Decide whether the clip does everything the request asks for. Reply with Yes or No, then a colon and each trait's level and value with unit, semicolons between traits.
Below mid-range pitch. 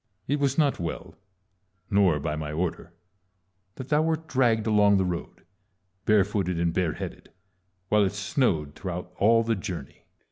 Yes: low, 100 Hz